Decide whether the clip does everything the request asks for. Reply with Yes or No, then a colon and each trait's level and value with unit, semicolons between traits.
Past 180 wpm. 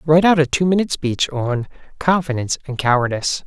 No: average, 175 wpm